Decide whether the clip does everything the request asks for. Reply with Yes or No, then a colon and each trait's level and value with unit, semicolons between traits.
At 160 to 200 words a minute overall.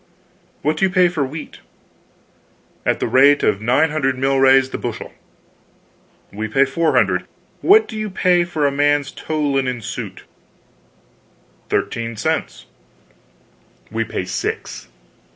No: slow, 135 wpm